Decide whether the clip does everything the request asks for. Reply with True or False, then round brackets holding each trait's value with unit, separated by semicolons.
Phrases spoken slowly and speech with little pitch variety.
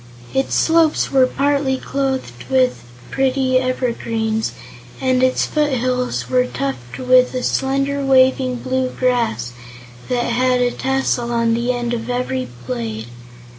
True (130 wpm; 2.2 semitones)